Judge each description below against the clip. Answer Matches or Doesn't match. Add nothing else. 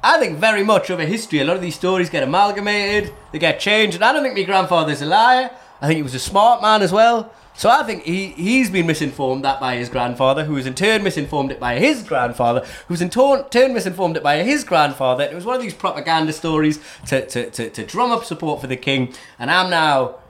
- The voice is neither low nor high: Matches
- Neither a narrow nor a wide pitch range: Doesn't match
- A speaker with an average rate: Doesn't match